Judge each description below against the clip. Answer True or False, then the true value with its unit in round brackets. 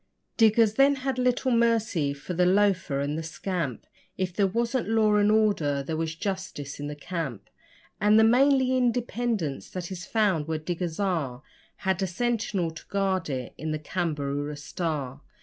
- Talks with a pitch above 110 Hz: True (185 Hz)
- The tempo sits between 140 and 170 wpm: True (165 wpm)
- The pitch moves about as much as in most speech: False (6.3 semitones)